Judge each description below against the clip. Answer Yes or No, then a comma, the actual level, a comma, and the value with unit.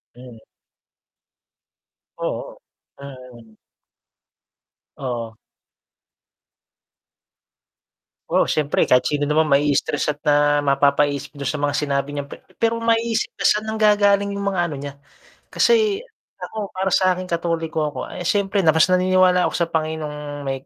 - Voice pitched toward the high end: No, medium, 155 Hz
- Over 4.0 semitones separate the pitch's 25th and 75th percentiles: Yes, average, 4.8 semitones